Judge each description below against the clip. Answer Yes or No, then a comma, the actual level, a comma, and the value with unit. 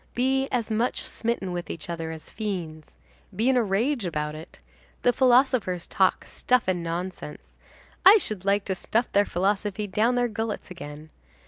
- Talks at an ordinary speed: Yes, average, 165 wpm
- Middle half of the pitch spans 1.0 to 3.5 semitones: No, wide, 5.4 semitones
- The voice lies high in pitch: Yes, high, 200 Hz